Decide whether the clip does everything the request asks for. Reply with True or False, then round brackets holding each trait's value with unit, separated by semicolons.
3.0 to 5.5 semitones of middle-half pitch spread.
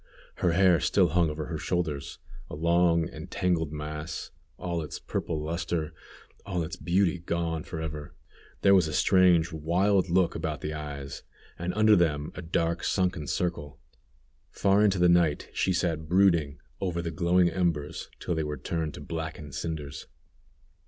False (2.5 semitones)